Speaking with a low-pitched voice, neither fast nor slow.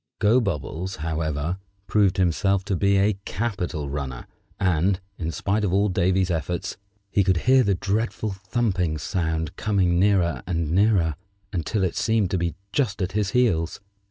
Yes: very low, 95 Hz; average, 155 wpm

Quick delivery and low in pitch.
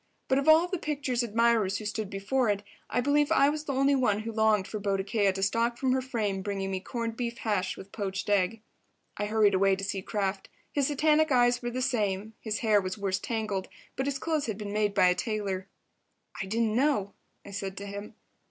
No: fast, 215 wpm; high, 215 Hz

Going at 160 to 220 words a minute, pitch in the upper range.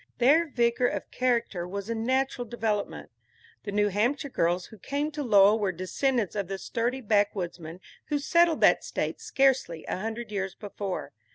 Yes: average, 165 wpm; high, 220 Hz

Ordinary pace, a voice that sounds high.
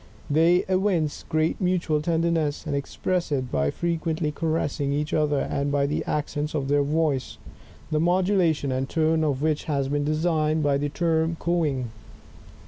No: average, 155 wpm; medium, 155 Hz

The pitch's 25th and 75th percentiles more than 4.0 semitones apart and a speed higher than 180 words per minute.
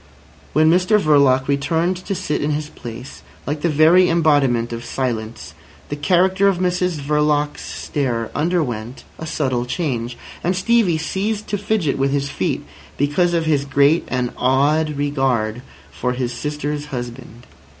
No: average, 4.7 semitones; average, 150 wpm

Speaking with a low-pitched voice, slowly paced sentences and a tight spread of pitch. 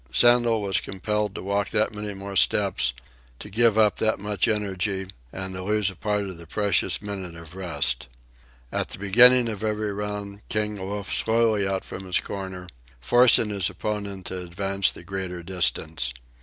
No: low, 100 Hz; average, 170 wpm; narrow, 2.1 semitones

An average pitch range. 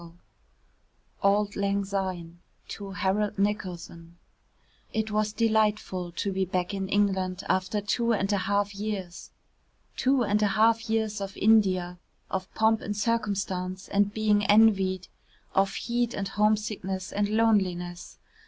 No: narrow, 2.1 semitones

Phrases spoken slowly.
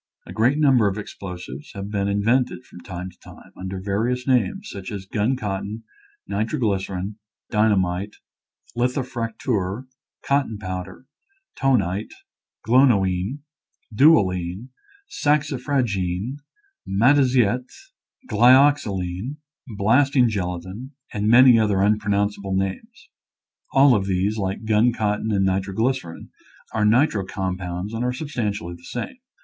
Yes: slow, 115 wpm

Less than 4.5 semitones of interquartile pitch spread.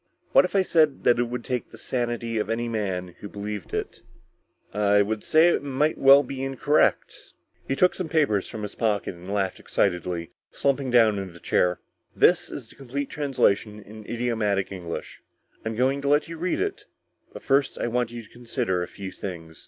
No: average, 5.3 semitones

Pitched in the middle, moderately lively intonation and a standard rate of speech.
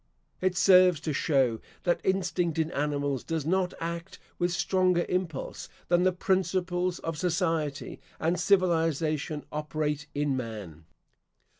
No: medium, 165 Hz; average, 3.4 semitones; slow, 125 wpm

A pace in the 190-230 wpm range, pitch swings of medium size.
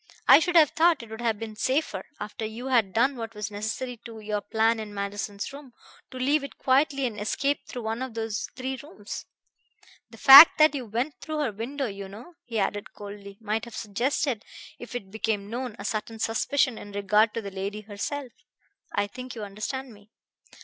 Yes: average, 200 wpm; average, 3.9 semitones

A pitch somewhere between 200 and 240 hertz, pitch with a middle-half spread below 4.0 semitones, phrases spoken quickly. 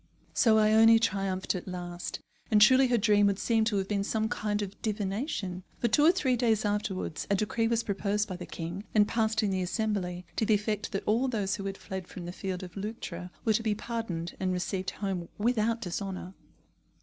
Yes: high, 205 Hz; average, 2.8 semitones; fast, 210 wpm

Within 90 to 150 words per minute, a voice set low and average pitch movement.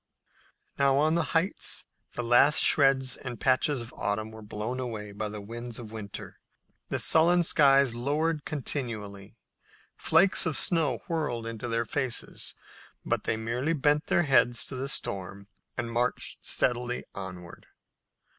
Yes: average, 145 wpm; low, 125 Hz; average, 4.8 semitones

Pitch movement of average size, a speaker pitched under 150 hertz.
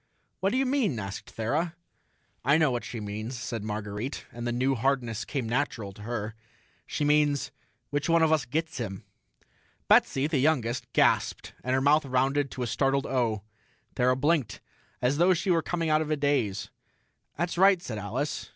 Yes: average, 4.8 semitones; low, 135 Hz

